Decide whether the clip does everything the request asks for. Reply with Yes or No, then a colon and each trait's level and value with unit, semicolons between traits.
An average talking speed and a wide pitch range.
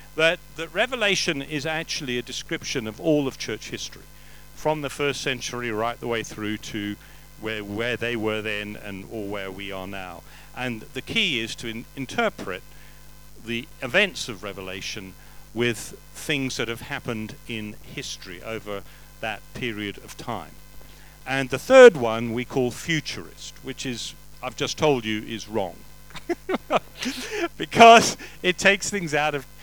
Yes: average, 155 wpm; wide, 5.7 semitones